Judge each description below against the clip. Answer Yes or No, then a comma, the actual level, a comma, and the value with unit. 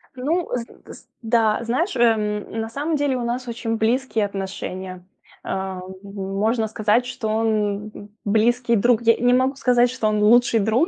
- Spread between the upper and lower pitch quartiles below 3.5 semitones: Yes, average, 2.9 semitones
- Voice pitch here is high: Yes, high, 225 Hz